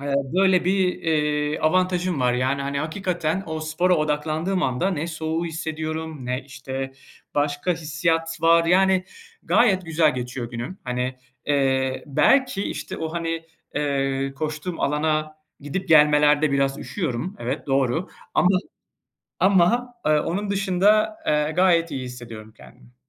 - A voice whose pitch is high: No, medium, 155 Hz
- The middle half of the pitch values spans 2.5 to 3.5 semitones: No, average, 4.3 semitones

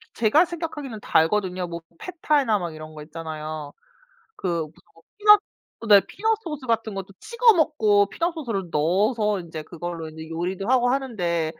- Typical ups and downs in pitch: No, wide, 8.5 semitones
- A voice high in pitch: Yes, high, 200 Hz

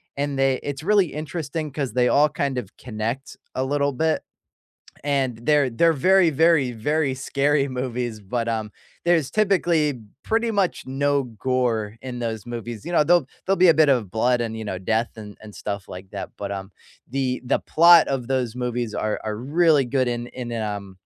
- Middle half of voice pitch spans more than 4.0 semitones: Yes, average, 4.5 semitones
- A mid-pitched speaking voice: No, low, 130 Hz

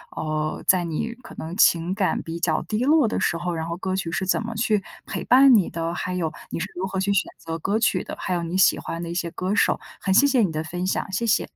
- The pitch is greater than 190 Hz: No, medium, 185 Hz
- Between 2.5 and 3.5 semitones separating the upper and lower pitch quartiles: No, average, 3.9 semitones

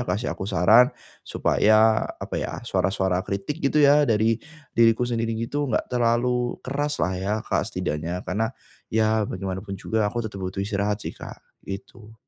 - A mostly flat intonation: No, average, 3.5 semitones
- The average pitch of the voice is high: No, low, 110 Hz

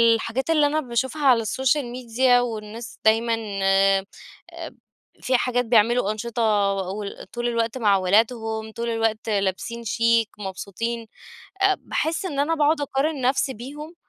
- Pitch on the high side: Yes, high, 235 Hz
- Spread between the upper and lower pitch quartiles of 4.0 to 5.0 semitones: No, average, 3.2 semitones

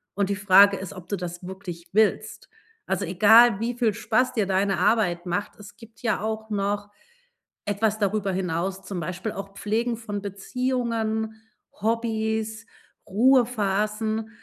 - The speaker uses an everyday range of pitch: No, narrow, 2.3 semitones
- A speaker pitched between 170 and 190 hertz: No, high, 210 Hz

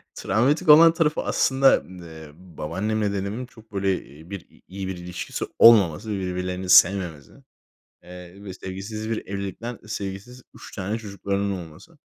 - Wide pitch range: No, average, 3.2 semitones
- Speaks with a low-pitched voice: Yes, low, 100 Hz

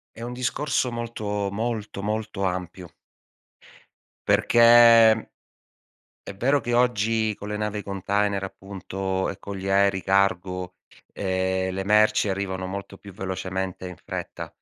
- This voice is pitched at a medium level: No, low, 100 Hz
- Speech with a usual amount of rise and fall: No, narrow, 2.2 semitones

